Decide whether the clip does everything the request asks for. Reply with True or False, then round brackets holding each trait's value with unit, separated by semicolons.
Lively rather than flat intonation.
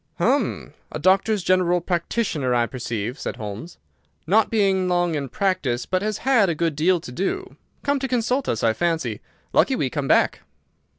True (6.4 semitones)